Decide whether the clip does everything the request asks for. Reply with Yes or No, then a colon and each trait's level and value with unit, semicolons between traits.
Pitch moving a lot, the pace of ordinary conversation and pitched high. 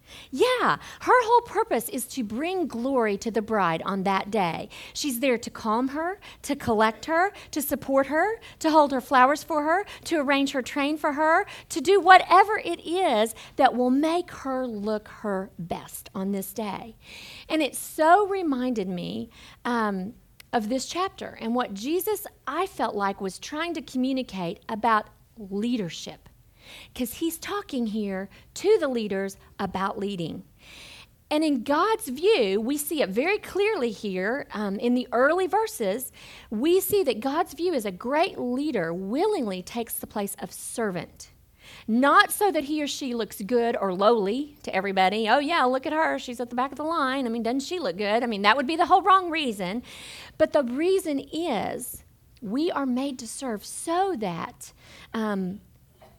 Yes: wide, 7.0 semitones; average, 175 wpm; very high, 260 Hz